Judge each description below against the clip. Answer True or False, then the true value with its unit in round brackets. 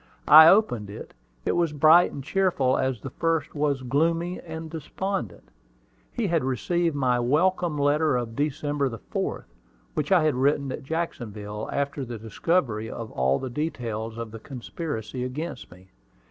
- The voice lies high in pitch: False (140 Hz)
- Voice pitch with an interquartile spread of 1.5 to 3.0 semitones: False (5.3 semitones)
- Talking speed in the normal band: True (155 wpm)